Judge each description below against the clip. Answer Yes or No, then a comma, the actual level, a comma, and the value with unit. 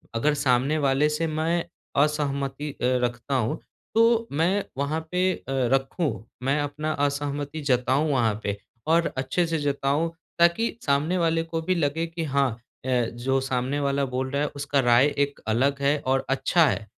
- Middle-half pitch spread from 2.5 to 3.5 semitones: Yes, average, 3.1 semitones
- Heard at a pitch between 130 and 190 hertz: Yes, medium, 140 Hz